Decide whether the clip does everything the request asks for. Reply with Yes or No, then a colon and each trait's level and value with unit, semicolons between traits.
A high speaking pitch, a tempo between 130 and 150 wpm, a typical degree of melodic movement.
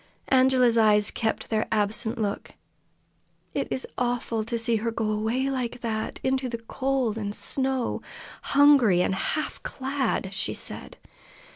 Yes: high, 235 Hz; average, 140 wpm; average, 3.2 semitones